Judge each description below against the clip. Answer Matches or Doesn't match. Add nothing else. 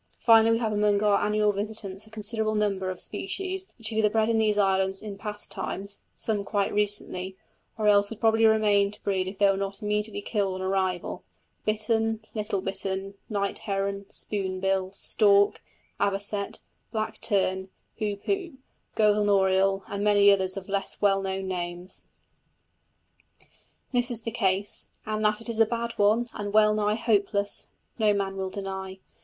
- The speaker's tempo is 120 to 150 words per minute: Doesn't match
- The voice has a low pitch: Doesn't match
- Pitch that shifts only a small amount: Matches